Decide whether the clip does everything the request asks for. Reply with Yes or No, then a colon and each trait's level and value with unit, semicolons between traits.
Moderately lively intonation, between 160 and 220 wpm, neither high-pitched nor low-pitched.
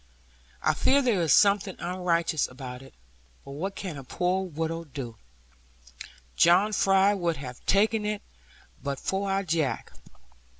No: average, 5.0 semitones; average, 140 wpm; medium, 175 Hz